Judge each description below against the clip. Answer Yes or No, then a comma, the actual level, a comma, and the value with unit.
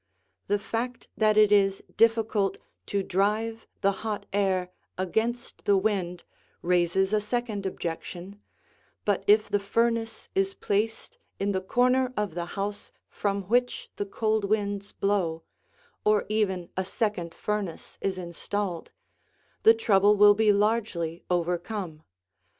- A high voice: Yes, high, 205 Hz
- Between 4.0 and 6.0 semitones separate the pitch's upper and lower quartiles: No, narrow, 2.5 semitones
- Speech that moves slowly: Yes, slow, 130 wpm